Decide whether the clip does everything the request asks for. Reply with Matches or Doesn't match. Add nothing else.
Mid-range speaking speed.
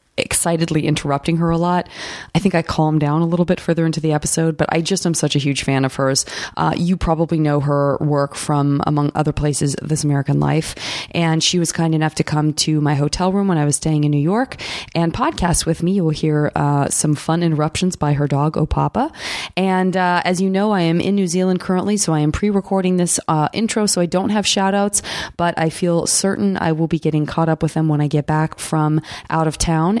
Doesn't match